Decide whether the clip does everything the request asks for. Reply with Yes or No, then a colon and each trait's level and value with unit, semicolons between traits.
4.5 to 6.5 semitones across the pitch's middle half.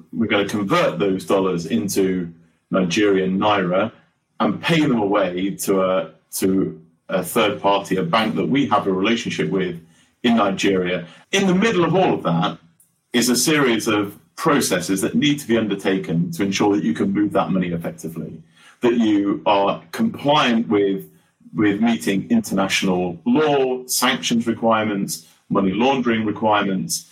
No: average, 4.1 semitones